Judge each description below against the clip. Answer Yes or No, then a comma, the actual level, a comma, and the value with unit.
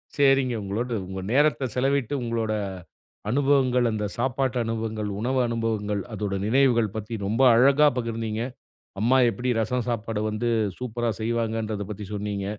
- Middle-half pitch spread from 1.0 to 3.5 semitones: Yes, average, 2.8 semitones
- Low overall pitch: Yes, low, 115 Hz